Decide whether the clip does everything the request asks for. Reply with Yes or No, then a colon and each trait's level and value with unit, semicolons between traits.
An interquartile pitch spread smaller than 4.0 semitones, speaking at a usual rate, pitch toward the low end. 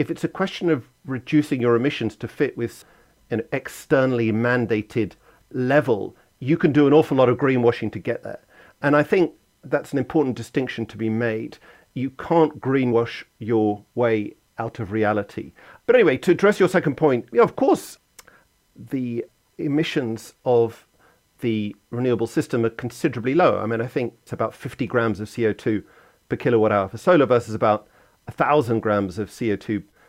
No: average, 4.4 semitones; average, 175 wpm; low, 120 Hz